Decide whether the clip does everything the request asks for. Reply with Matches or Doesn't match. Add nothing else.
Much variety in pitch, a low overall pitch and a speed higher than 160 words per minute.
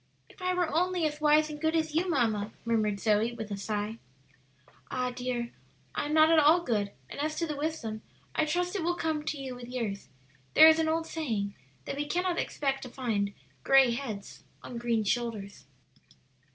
Doesn't match